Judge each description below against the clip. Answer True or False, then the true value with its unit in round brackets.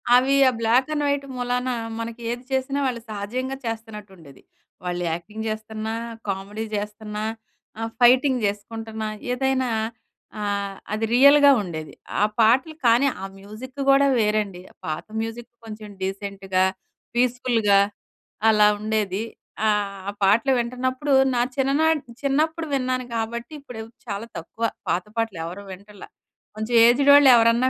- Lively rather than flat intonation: False (3.8 semitones)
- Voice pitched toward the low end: False (225 Hz)